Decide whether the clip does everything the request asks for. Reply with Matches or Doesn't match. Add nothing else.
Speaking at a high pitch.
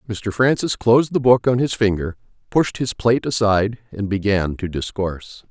Doesn't match